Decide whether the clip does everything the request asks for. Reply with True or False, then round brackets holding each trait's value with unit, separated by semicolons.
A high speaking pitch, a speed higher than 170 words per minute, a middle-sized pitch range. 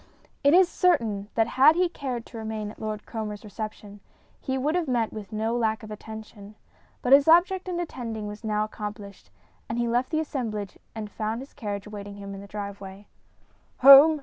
True (220 Hz; 190 wpm; 4.5 semitones)